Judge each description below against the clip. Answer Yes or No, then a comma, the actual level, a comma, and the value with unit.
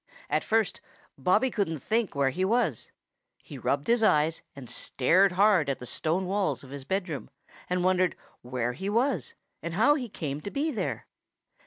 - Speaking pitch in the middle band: Yes, medium, 180 Hz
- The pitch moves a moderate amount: No, wide, 7.0 semitones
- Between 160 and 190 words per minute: Yes, average, 175 wpm